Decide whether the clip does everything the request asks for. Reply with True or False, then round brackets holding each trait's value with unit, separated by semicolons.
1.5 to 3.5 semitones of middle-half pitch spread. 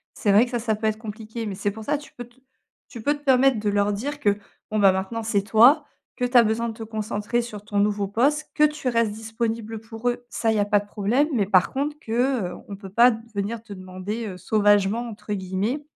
True (2.8 semitones)